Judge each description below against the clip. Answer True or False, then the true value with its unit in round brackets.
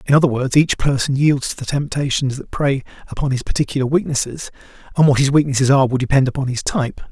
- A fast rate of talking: True (210 wpm)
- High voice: False (135 Hz)